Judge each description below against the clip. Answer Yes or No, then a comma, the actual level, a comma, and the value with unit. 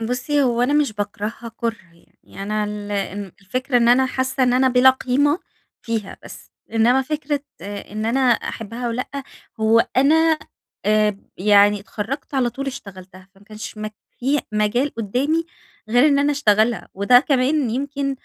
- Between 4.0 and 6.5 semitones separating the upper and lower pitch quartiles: Yes, average, 4.3 semitones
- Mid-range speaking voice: No, high, 245 Hz